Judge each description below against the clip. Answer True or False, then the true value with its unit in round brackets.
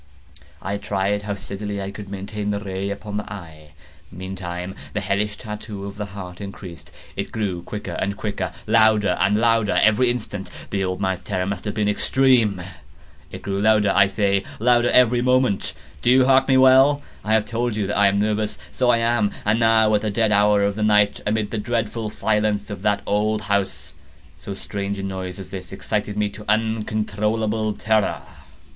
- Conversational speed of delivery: True (190 wpm)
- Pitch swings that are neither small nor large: False (1.9 semitones)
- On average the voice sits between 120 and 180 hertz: False (105 Hz)